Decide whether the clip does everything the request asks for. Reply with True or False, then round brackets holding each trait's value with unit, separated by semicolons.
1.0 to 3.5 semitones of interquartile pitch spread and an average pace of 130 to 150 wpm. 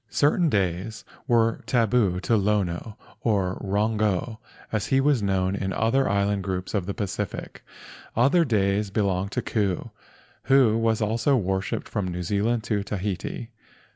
True (2.9 semitones; 140 wpm)